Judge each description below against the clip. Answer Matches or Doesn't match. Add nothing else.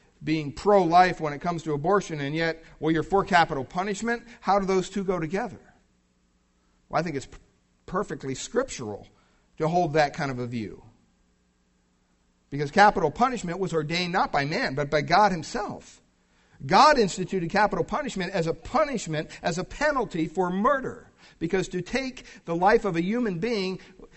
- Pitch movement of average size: Doesn't match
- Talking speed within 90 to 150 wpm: Doesn't match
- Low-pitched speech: Doesn't match